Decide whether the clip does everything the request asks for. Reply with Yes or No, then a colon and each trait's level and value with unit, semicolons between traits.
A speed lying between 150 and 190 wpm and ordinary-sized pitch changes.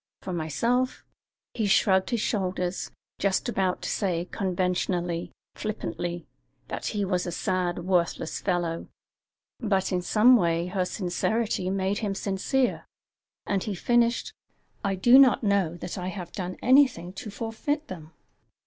No: average, 140 wpm; average, 3.4 semitones